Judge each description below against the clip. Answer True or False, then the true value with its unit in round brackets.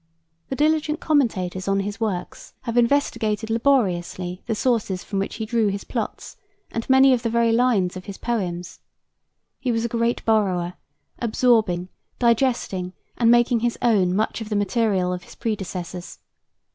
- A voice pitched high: True (220 Hz)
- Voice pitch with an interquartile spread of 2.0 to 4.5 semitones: True (4.2 semitones)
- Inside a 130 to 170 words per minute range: True (160 wpm)